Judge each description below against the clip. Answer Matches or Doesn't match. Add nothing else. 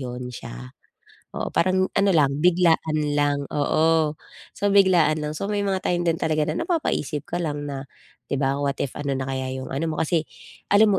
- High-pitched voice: Doesn't match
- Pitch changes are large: Doesn't match